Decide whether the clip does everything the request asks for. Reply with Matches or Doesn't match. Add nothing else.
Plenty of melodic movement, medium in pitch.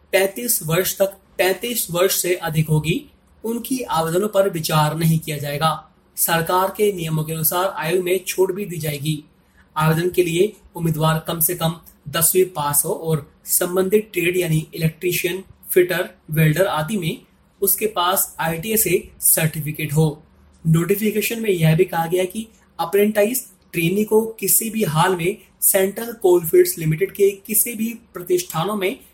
Doesn't match